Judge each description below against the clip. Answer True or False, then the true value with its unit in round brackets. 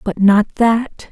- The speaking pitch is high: True (215 Hz)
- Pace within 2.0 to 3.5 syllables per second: True (3.0 syllables/s)